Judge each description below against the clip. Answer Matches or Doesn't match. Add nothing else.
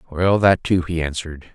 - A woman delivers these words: Doesn't match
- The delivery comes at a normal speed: Matches